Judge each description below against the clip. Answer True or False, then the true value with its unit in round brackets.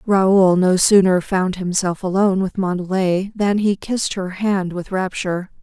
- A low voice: False (190 Hz)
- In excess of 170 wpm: False (160 wpm)